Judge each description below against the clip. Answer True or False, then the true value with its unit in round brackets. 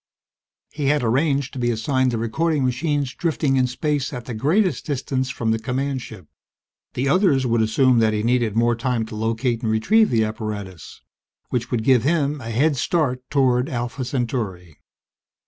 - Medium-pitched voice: False (125 Hz)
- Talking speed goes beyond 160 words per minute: True (175 wpm)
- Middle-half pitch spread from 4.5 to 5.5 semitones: False (3.6 semitones)